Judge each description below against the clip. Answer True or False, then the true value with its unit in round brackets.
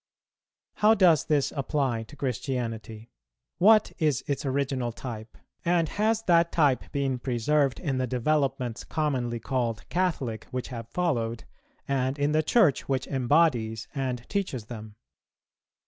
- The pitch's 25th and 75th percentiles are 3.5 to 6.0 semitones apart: True (4.3 semitones)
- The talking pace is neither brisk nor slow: False (130 wpm)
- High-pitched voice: False (135 Hz)